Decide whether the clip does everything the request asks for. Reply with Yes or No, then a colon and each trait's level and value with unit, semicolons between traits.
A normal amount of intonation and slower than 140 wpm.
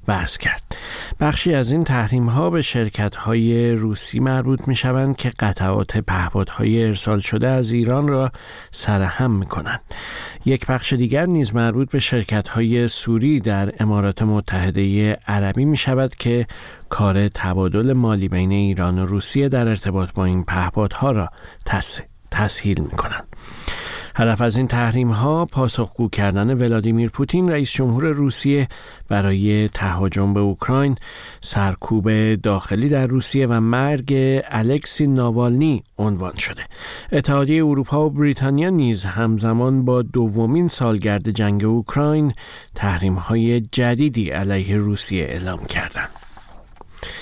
Yes: average, 4.6 semitones; average, 130 wpm